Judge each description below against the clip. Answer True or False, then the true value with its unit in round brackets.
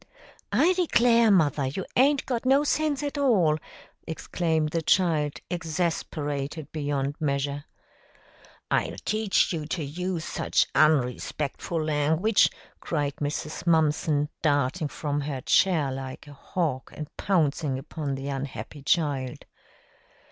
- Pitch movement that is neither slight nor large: True (4.0 semitones)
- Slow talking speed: True (120 wpm)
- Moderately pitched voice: True (155 Hz)